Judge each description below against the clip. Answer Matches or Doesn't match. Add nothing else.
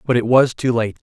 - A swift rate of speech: Matches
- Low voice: Matches